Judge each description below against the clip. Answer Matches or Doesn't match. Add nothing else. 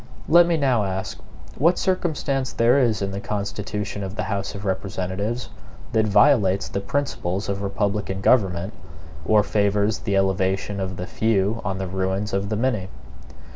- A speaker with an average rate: Matches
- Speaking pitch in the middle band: Doesn't match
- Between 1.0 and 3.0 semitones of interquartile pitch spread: Matches